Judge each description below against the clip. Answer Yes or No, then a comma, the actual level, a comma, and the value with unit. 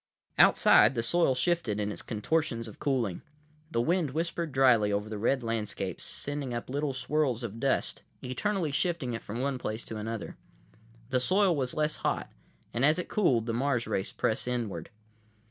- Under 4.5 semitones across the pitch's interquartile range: No, average, 4.8 semitones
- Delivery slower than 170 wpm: No, average, 180 wpm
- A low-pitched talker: Yes, low, 125 Hz